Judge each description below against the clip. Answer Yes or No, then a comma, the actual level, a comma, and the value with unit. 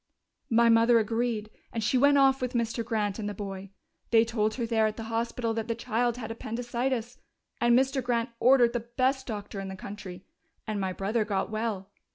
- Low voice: No, high, 230 Hz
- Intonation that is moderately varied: No, narrow, 2.2 semitones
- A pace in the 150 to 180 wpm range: No, average, 200 wpm